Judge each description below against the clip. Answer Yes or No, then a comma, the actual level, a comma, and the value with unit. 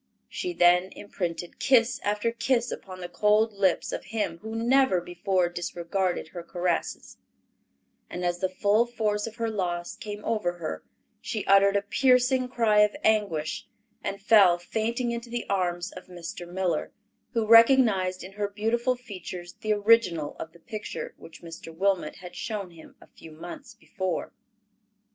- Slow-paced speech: No, average, 155 wpm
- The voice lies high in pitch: Yes, high, 200 Hz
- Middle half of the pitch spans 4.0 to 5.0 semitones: Yes, average, 4.4 semitones